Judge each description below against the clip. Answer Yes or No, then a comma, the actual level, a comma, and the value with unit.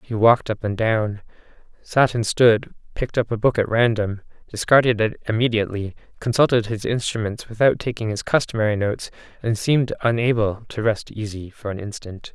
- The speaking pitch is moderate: No, low, 110 Hz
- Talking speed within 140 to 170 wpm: Yes, average, 165 wpm